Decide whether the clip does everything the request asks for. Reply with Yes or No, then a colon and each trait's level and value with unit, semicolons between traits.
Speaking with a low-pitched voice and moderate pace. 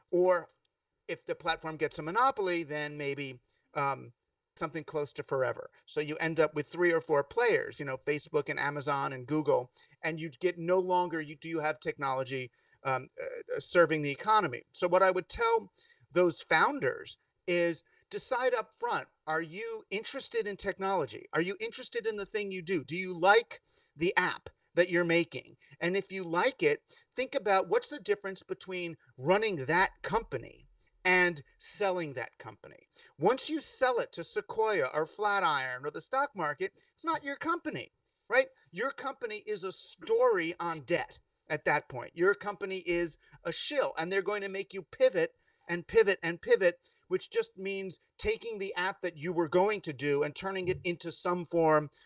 No: medium, 185 Hz; average, 180 wpm